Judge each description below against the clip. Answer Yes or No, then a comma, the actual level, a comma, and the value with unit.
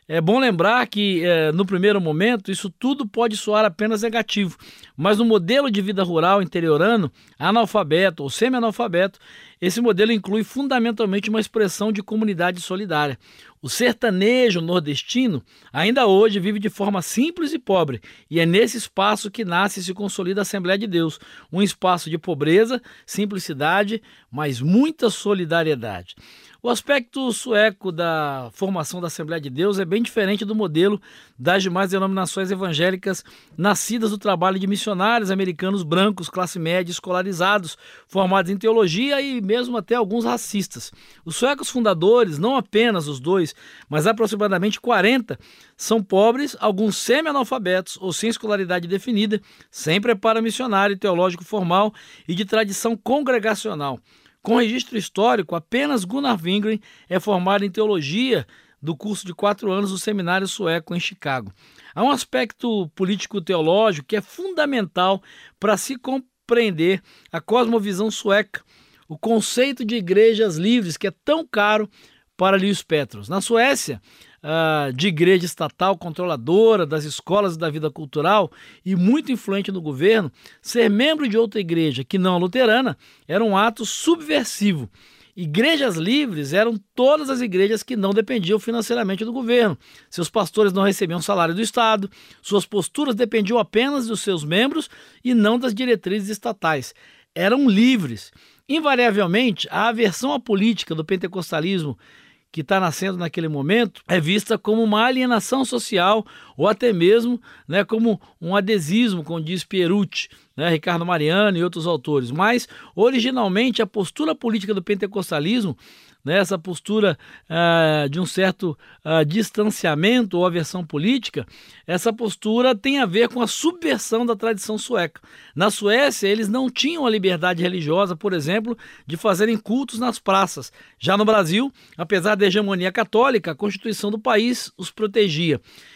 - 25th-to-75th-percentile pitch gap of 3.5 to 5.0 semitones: Yes, average, 4.1 semitones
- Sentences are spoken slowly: No, average, 145 wpm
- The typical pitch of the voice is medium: No, high, 205 Hz